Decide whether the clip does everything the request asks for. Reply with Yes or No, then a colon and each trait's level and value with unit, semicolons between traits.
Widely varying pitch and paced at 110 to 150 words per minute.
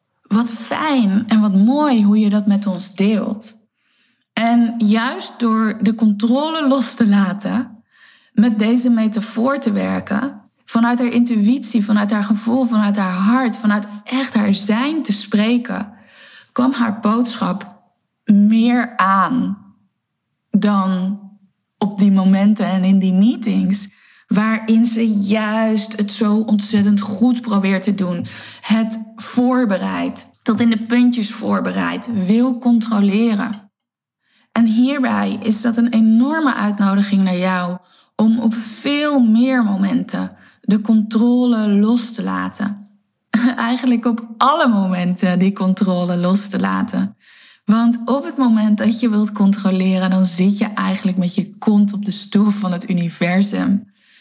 No: average, 2.7 semitones; slow, 135 wpm